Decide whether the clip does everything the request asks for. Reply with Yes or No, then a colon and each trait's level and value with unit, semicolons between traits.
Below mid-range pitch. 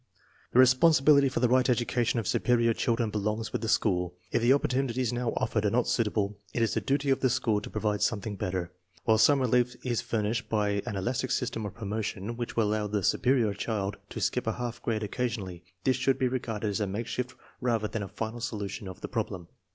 Yes: low, 115 Hz